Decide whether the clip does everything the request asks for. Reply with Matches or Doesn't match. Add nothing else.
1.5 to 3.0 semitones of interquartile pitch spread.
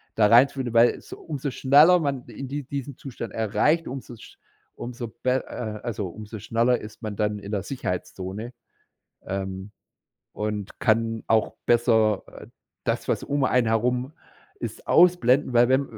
Doesn't match